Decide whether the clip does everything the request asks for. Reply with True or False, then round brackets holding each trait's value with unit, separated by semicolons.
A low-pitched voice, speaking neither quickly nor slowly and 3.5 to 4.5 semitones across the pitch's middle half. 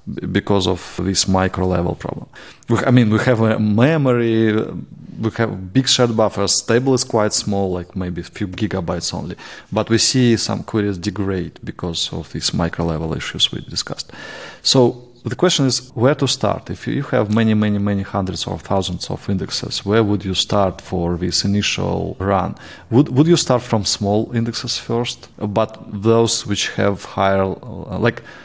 True (105 Hz; 170 wpm; 3.8 semitones)